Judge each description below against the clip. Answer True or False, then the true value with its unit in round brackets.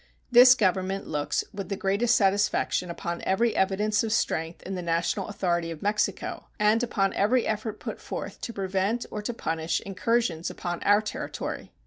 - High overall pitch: True (195 Hz)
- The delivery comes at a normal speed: True (165 wpm)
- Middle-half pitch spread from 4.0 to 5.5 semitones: False (3.2 semitones)